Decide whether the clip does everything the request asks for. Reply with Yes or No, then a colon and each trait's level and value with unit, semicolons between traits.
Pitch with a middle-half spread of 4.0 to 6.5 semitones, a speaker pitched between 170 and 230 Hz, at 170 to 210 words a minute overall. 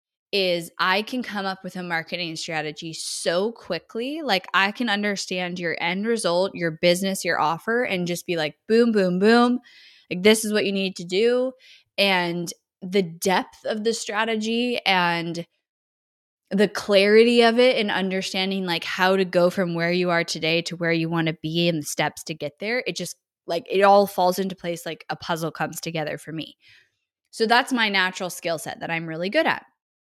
No: average, 3.5 semitones; medium, 185 Hz; average, 195 wpm